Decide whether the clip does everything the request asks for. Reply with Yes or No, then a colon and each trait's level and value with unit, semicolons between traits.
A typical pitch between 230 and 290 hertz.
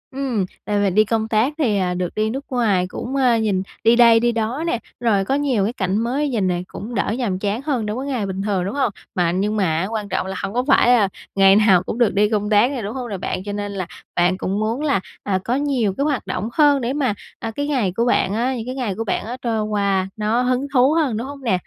No: high, 220 Hz